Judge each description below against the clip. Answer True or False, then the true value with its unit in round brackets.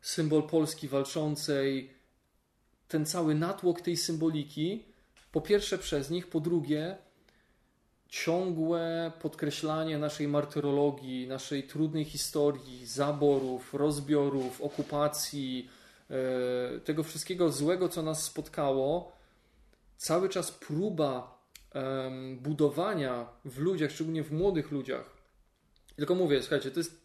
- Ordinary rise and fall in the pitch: True (3.1 semitones)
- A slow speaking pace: True (100 wpm)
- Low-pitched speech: False (150 Hz)